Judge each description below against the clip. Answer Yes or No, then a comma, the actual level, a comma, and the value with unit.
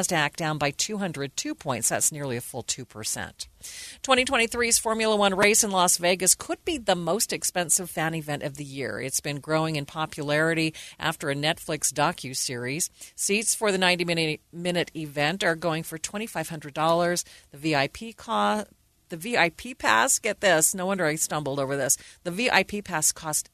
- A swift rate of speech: No, average, 160 wpm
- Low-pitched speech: No, medium, 160 Hz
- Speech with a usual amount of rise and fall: Yes, average, 4.7 semitones